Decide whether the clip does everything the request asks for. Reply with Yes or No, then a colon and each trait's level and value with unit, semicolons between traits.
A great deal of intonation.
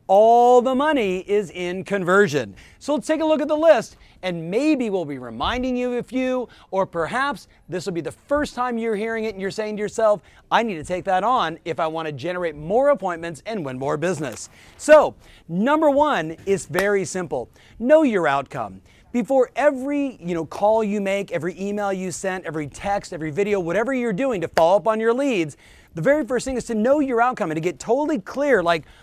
Yes: wide, 6.1 semitones